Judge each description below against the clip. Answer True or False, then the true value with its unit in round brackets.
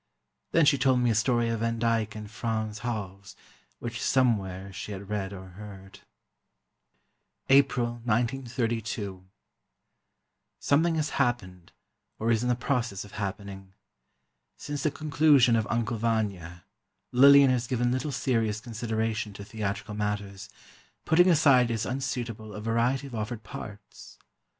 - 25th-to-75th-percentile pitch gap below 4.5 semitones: True (3.2 semitones)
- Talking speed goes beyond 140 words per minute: False (135 wpm)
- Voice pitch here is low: True (115 Hz)